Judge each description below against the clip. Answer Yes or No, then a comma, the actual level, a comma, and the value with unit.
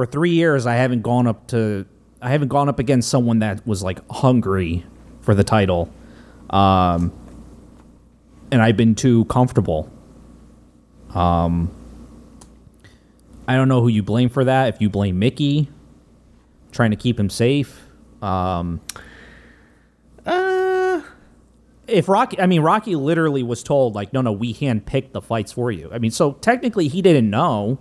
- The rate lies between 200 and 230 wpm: No, average, 155 wpm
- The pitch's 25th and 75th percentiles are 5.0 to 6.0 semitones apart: Yes, wide, 5.4 semitones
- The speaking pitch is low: Yes, low, 120 Hz